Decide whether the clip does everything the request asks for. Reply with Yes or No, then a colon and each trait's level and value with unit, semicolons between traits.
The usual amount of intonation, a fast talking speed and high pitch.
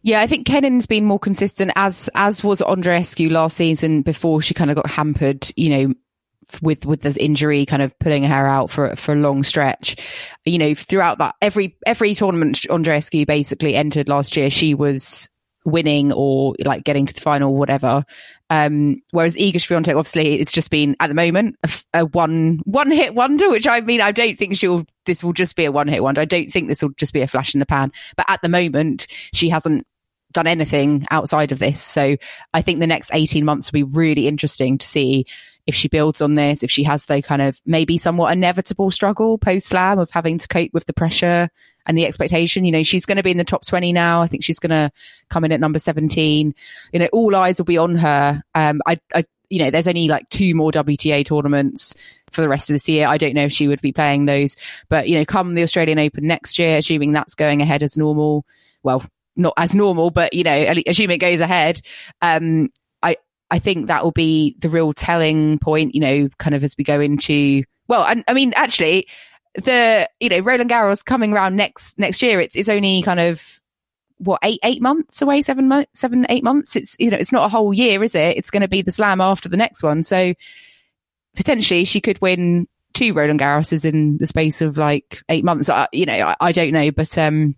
No: average, 4.0 semitones; fast, 225 wpm; medium, 160 Hz